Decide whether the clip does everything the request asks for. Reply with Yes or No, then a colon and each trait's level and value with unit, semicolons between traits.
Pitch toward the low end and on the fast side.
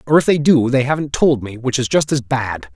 Yes: low, 130 Hz; fast, 285 wpm